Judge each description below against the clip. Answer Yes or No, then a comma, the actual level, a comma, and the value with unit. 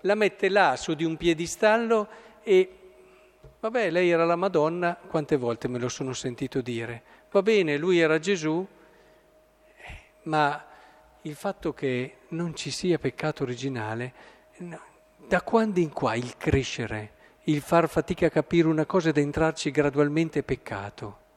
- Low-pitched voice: No, medium, 155 Hz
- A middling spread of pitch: Yes, average, 4.8 semitones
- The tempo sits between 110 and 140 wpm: No, average, 150 wpm